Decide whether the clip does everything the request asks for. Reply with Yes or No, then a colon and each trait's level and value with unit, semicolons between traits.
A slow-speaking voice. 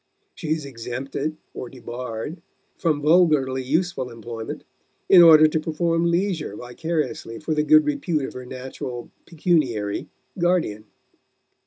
Yes: slow, 125 wpm